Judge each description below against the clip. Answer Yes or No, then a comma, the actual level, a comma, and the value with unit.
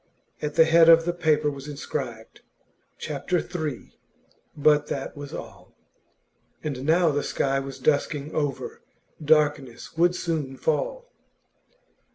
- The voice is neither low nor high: Yes, medium, 150 Hz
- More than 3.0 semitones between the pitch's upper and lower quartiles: No, narrow, 2.6 semitones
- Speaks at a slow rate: Yes, slow, 125 wpm